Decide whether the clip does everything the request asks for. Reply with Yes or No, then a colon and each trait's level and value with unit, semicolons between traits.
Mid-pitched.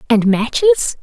No: high, 245 Hz